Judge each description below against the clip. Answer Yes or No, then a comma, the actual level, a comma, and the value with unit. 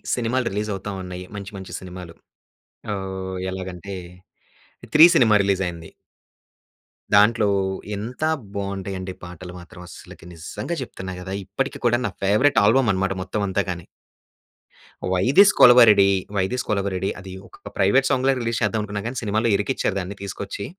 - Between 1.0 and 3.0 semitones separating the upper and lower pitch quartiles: No, average, 3.4 semitones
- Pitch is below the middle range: Yes, low, 100 Hz